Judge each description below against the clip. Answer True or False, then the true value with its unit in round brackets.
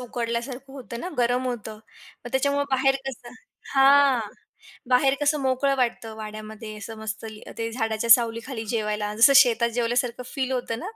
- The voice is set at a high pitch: True (240 Hz)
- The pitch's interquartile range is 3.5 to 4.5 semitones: False (2.9 semitones)